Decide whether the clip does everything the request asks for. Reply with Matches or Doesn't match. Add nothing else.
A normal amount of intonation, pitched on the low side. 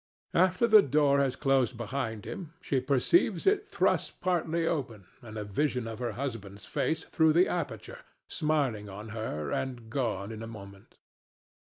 Doesn't match